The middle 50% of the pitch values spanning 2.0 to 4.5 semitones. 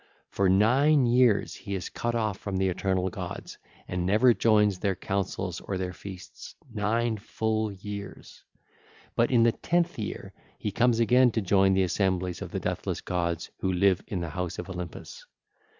Yes: average, 3.6 semitones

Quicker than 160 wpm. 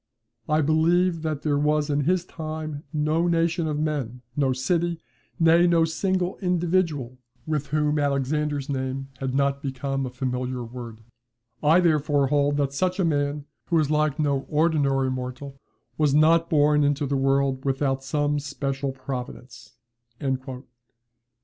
No: average, 145 wpm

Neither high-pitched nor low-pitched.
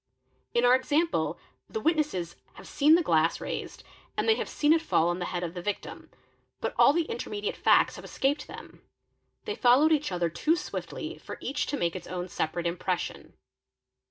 No: high, 245 Hz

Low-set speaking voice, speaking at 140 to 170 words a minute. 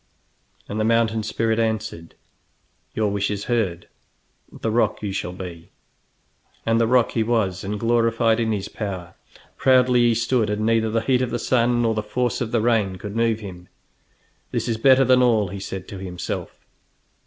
No: low, 110 Hz; average, 180 wpm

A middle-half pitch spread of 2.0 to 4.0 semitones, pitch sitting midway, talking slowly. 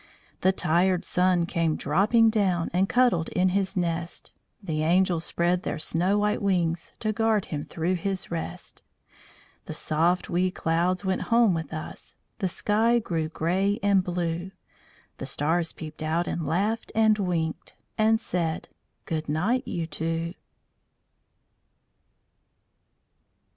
Yes: average, 3.4 semitones; medium, 180 Hz; slow, 130 wpm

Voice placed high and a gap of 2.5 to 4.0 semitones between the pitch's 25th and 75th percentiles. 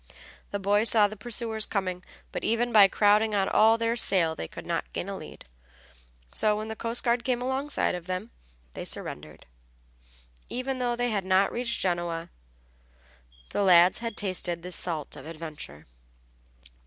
No: high, 205 Hz; average, 4.6 semitones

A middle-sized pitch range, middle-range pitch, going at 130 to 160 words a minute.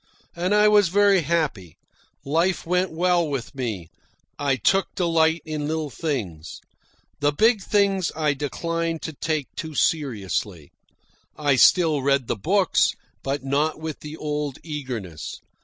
Yes: average, 3.8 semitones; medium, 155 Hz; average, 140 wpm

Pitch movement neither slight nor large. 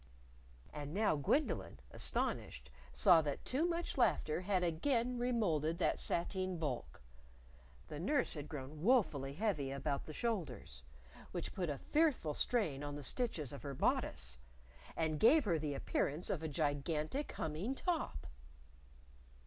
No: wide, 7.8 semitones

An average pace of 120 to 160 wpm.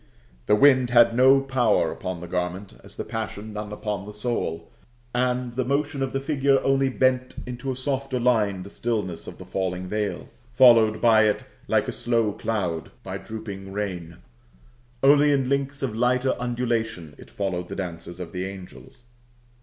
No: average, 170 wpm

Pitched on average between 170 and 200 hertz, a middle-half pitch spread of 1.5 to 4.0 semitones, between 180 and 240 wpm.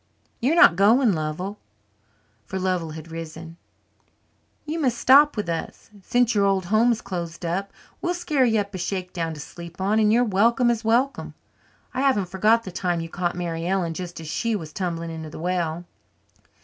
No: high, 190 Hz; average, 5.2 semitones; average, 185 wpm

